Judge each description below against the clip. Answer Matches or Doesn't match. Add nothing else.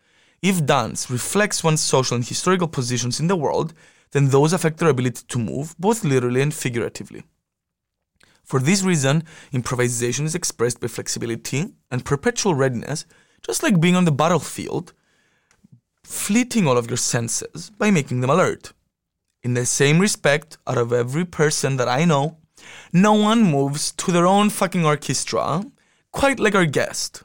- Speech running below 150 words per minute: Doesn't match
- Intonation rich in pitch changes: Matches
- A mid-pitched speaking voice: Matches